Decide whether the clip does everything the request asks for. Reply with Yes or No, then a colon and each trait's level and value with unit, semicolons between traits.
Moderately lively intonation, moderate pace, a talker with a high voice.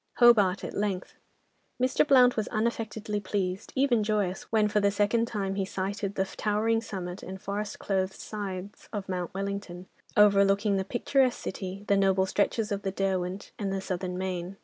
No: narrow, 2.0 semitones; average, 170 wpm; high, 200 Hz